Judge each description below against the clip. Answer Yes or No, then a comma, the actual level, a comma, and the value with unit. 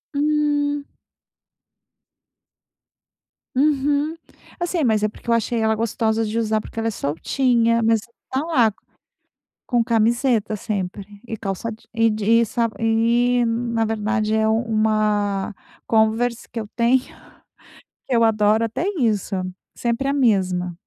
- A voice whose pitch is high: Yes, high, 225 Hz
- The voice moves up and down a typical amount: No, narrow, 2.1 semitones